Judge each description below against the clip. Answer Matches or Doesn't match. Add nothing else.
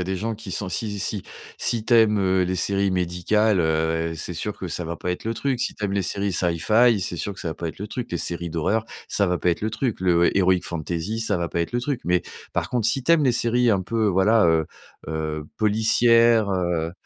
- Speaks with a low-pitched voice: Matches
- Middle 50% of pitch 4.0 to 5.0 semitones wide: Matches